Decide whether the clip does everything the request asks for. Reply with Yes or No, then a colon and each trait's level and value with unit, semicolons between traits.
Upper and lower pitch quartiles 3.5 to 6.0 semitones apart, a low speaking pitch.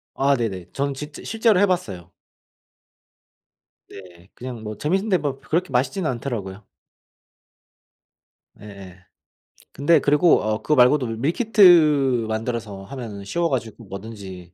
No: wide, 6.7 semitones; low, 125 Hz